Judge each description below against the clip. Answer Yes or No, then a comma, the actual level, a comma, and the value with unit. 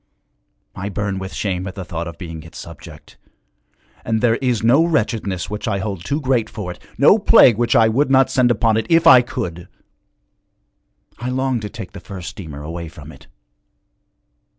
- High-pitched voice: No, low, 105 Hz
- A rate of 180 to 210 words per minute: Yes, average, 185 wpm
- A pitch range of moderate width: No, wide, 5.8 semitones